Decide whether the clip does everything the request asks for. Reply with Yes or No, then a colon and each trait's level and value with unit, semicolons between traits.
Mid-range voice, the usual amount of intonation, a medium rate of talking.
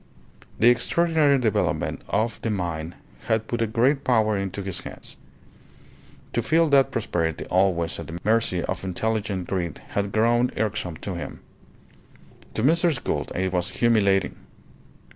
No: low, 105 Hz; average, 4.5 semitones; average, 145 wpm